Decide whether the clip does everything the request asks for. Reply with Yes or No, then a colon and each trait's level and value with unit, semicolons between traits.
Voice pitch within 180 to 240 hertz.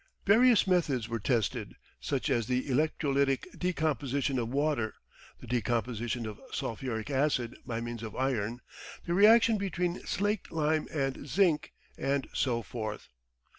No: low, 135 Hz